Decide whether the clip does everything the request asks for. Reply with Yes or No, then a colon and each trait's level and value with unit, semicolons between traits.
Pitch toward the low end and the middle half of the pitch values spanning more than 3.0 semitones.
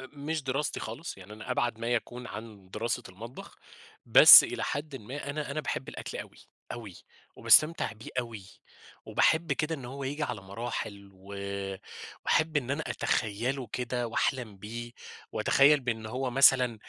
Yes: low, 120 Hz; average, 4.2 semitones